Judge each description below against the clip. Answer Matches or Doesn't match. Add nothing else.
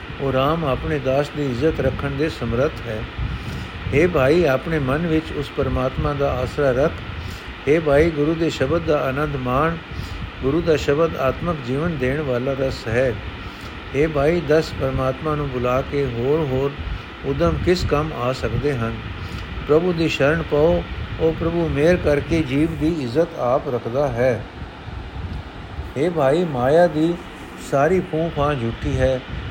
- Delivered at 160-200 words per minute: Doesn't match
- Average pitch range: Matches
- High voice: Doesn't match